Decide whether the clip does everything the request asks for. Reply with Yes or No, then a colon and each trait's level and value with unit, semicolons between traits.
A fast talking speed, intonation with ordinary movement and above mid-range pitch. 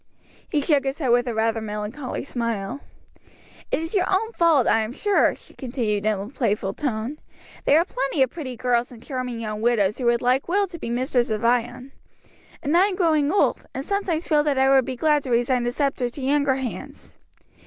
Yes: fast, 210 wpm; average, 4.1 semitones; very high, 260 Hz